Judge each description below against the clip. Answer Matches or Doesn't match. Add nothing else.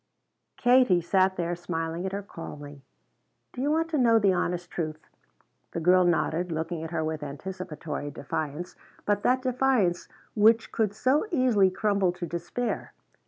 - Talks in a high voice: Doesn't match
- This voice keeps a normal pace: Matches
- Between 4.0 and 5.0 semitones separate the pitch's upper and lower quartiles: Doesn't match